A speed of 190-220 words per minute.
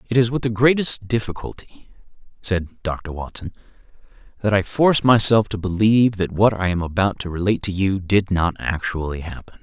No: average, 175 wpm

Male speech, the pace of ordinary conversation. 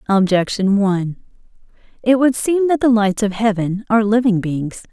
No: female; average, 160 wpm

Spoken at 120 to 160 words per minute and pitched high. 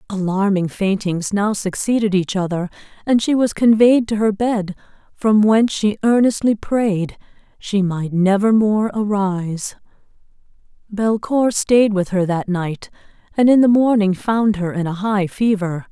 Yes: average, 145 wpm; high, 205 Hz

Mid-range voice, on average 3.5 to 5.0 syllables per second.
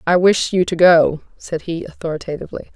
No: medium, 170 Hz; 5.7 syllables/s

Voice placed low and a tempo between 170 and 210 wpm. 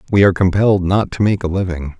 No: very low, 95 Hz; fast, 240 wpm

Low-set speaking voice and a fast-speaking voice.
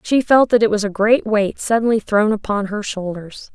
No: high, 210 Hz; fast, 220 wpm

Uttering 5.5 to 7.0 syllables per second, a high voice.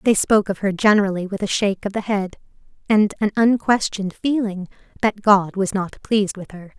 Yes: 5.6 syllables/s; high, 200 Hz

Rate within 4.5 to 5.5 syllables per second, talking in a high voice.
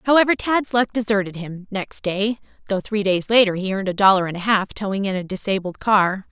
No: 5.7 syllables/s; high, 200 Hz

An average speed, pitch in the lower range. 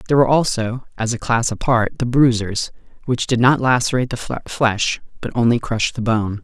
Yes: average, 185 wpm; low, 120 Hz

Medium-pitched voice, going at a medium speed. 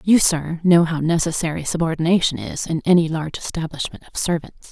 Yes: medium, 165 Hz; average, 165 wpm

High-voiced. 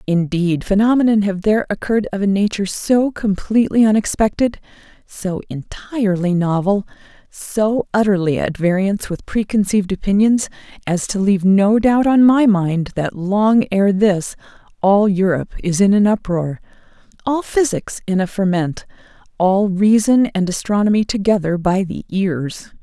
Yes: high, 200 Hz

